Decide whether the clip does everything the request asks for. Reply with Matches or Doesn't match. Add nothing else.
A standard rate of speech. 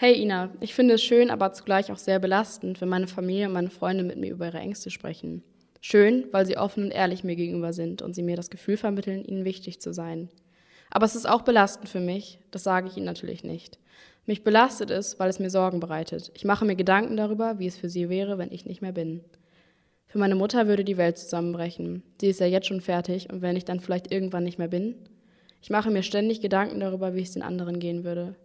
Doesn't match